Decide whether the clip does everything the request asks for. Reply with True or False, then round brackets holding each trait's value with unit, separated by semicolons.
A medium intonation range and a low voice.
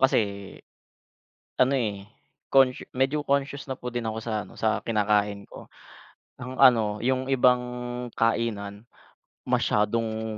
True (3.5 semitones; 115 Hz)